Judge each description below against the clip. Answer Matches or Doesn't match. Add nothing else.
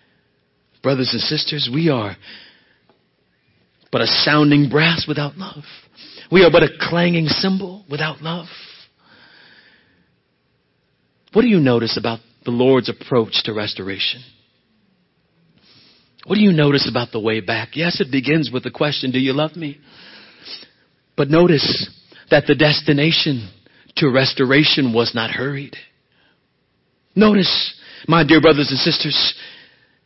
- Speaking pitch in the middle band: Matches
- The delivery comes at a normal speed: Doesn't match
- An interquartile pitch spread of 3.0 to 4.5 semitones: Matches